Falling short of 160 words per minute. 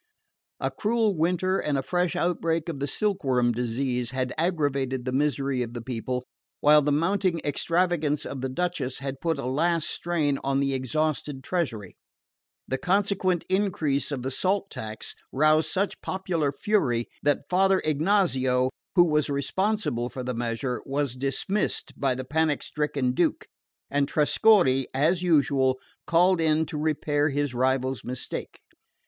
Yes: average, 150 wpm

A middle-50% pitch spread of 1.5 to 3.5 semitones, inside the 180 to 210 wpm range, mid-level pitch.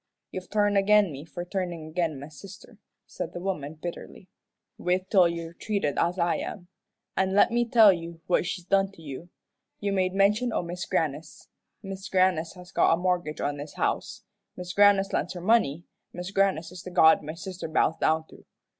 Yes: average, 3.0 semitones; average, 190 wpm; medium, 180 Hz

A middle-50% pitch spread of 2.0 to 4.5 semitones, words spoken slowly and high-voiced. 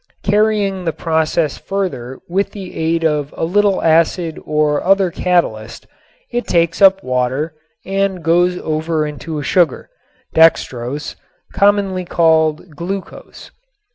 No: average, 3.8 semitones; slow, 120 wpm; medium, 165 Hz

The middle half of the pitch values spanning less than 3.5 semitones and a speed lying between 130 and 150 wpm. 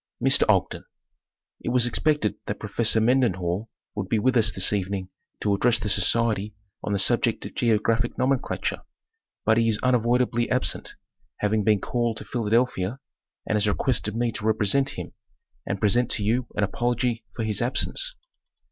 No: average, 2.7 semitones; average, 165 wpm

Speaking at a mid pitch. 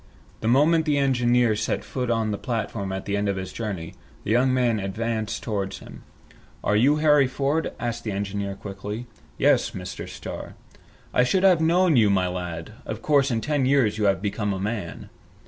No: low, 115 Hz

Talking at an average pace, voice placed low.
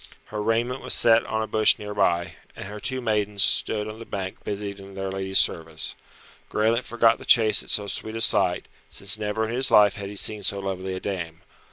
No: fast, 220 wpm; low, 105 Hz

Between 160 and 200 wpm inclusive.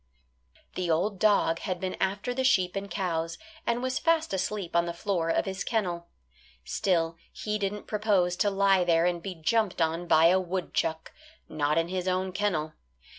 Yes: average, 175 wpm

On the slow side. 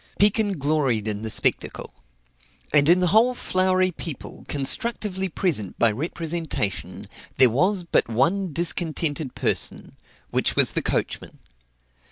Yes: slow, 125 wpm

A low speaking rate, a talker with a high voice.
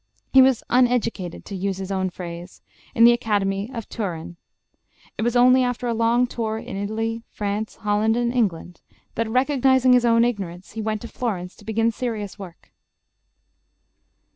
No: average, 165 wpm; high, 220 Hz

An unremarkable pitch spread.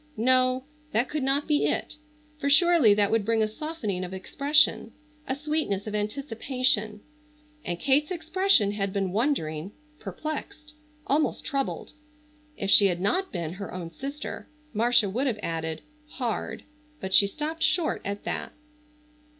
No: wide, 6.7 semitones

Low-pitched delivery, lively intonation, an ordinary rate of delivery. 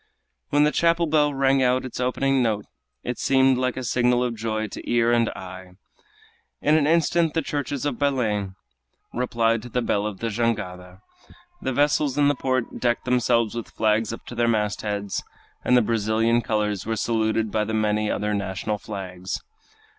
No: low, 115 Hz; average, 3.6 semitones; average, 175 wpm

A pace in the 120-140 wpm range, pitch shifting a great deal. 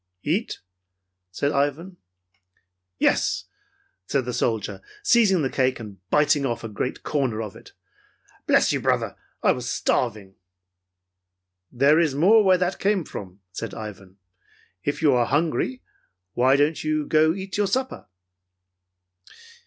Yes: slow, 135 wpm; wide, 6.9 semitones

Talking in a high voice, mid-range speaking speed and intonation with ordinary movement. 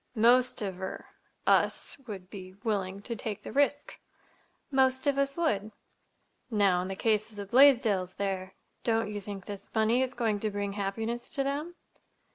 Yes: high, 215 Hz; average, 155 wpm; average, 4.4 semitones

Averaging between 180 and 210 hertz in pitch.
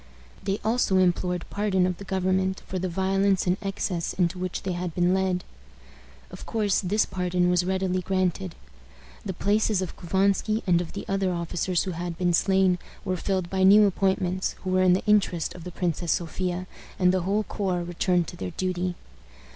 Yes: medium, 185 Hz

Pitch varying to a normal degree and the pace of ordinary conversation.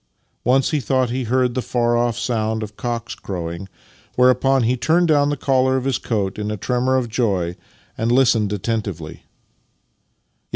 Yes: average, 3.4 semitones; average, 170 wpm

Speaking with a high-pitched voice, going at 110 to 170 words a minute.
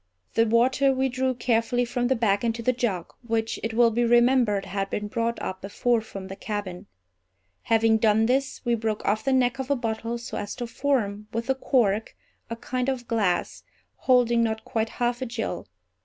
No: high, 230 Hz; average, 195 wpm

